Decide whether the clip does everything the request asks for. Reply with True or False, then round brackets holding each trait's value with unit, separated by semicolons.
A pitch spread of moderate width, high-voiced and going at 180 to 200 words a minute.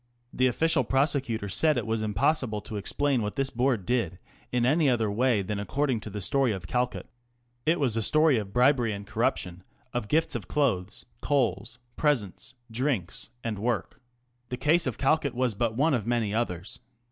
False (4.6 semitones; 120 Hz; 185 wpm)